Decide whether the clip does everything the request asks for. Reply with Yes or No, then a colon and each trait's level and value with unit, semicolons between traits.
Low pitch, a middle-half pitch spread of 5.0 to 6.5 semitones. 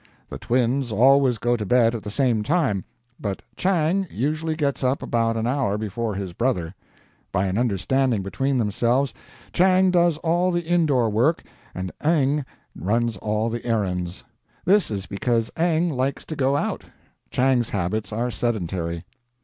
Yes: low, 120 Hz; wide, 5.4 semitones